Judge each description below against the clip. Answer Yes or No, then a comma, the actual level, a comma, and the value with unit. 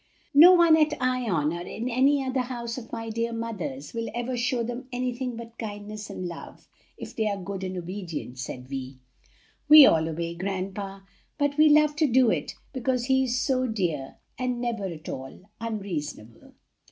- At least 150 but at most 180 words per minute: Yes, average, 175 wpm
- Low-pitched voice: No, high, 230 Hz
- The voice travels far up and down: Yes, wide, 5.7 semitones